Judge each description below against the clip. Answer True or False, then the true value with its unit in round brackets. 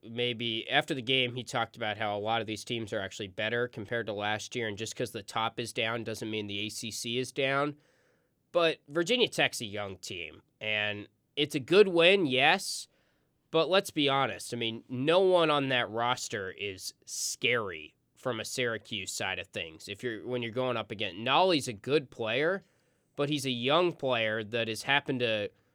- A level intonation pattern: False (4.0 semitones)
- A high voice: False (120 Hz)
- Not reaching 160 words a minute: False (195 wpm)